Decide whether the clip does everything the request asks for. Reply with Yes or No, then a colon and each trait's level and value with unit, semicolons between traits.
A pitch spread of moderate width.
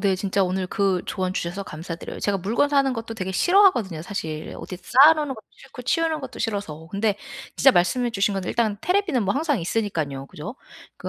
No: wide, 5.9 semitones